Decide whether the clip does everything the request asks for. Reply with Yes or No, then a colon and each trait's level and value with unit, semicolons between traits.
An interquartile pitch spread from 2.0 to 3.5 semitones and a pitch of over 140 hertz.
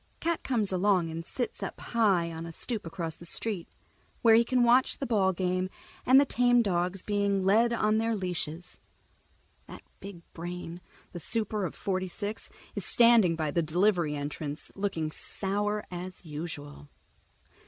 No: average, 4.5 semitones; high, 190 Hz